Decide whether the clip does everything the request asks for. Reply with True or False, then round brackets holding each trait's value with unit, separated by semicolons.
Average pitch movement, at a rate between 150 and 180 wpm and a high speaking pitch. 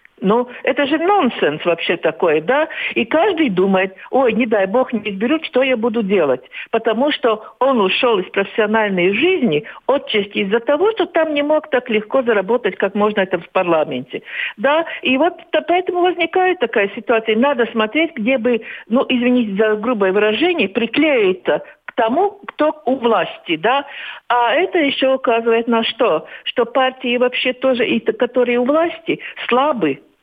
False (5.8 semitones; 160 wpm; 250 Hz)